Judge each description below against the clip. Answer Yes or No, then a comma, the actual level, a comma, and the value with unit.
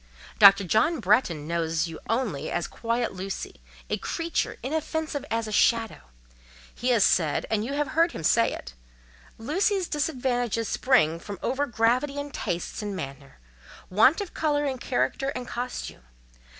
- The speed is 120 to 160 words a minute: Yes, average, 145 wpm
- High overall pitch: Yes, high, 230 Hz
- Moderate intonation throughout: No, wide, 7.6 semitones